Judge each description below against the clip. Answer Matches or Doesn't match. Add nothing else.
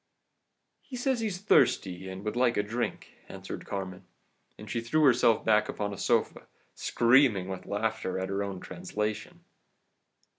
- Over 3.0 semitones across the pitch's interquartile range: Matches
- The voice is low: Matches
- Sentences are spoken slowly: Doesn't match